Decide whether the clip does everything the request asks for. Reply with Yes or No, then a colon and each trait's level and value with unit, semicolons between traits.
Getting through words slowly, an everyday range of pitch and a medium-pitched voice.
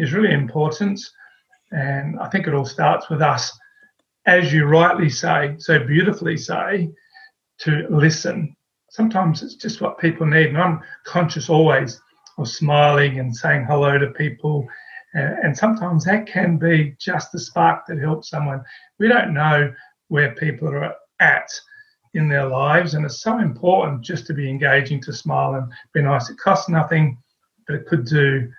No: average, 165 wpm; average, 3.9 semitones; medium, 155 Hz